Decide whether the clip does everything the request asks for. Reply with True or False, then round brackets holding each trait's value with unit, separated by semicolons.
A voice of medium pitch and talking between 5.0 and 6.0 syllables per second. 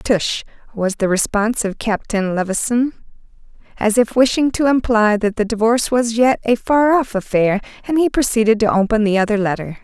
False (225 Hz; 5.3 syllables/s)